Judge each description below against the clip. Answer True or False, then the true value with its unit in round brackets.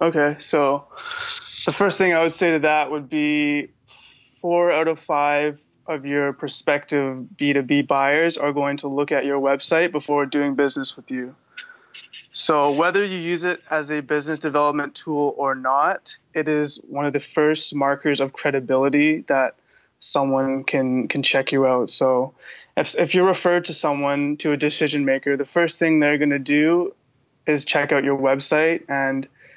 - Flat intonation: True (2.2 semitones)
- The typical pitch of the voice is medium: True (145 Hz)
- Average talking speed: True (170 wpm)